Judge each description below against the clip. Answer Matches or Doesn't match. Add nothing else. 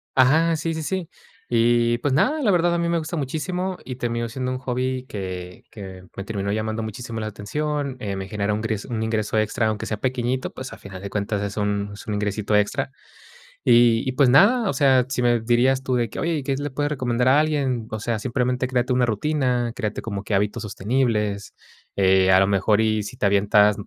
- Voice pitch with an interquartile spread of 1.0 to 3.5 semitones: Doesn't match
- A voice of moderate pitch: Doesn't match